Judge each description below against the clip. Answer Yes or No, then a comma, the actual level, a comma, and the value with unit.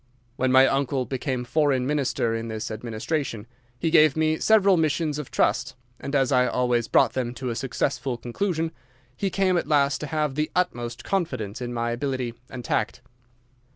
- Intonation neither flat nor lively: Yes, average, 4.3 semitones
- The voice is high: No, low, 135 Hz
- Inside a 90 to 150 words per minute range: No, average, 175 wpm